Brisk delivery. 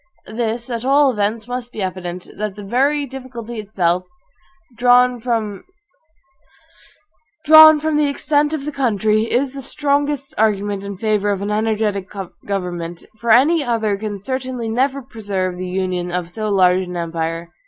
No: average, 145 wpm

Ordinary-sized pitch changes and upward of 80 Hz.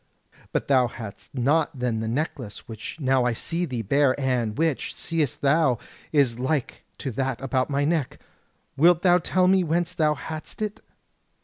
Yes: average, 4.5 semitones; medium, 140 Hz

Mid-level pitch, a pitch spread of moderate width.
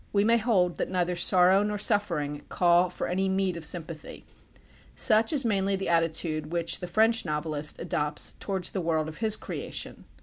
Yes: medium, 180 Hz; average, 3.6 semitones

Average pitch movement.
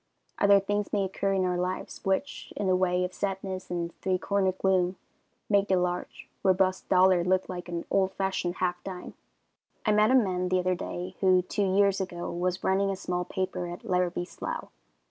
No: narrow, 1.3 semitones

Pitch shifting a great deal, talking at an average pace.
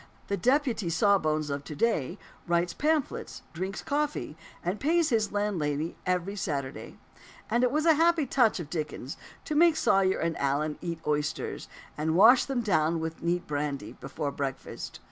Yes: wide, 7.9 semitones; average, 160 wpm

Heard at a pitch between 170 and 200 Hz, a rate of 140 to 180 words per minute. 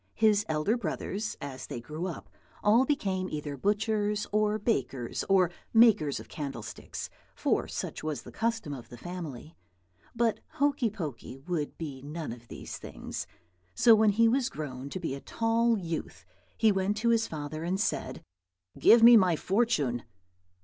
Yes: medium, 185 Hz; average, 165 wpm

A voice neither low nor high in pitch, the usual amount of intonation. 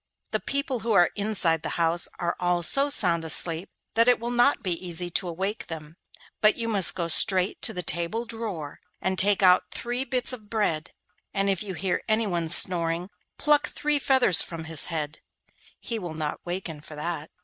Yes: medium, 180 Hz; average, 5.0 semitones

